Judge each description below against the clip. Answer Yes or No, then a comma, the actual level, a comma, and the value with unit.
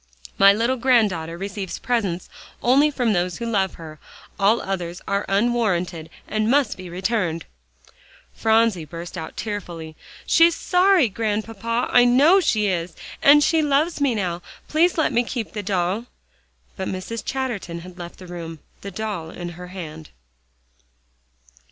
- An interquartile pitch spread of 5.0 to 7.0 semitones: Yes, average, 5.3 semitones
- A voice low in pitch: No, high, 205 Hz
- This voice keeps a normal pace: Yes, average, 145 wpm